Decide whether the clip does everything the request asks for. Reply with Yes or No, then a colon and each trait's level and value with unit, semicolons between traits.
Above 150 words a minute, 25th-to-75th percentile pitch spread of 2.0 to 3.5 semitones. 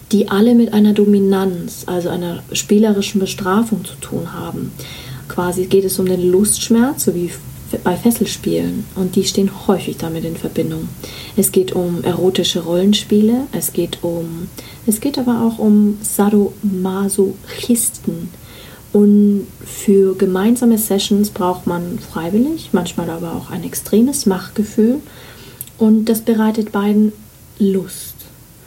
No: average, 130 wpm; average, 3.0 semitones